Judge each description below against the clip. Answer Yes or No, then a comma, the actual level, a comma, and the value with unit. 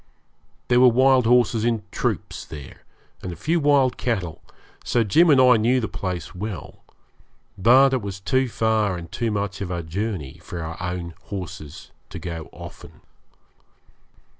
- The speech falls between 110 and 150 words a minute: No, average, 160 wpm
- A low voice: Yes, low, 105 Hz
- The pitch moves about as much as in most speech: No, wide, 5.7 semitones